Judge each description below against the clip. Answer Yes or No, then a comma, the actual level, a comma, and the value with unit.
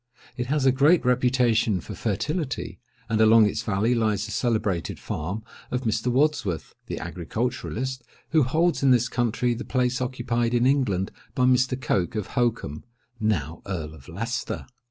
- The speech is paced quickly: No, average, 155 wpm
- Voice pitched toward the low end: Yes, low, 120 Hz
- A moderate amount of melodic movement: Yes, average, 3.4 semitones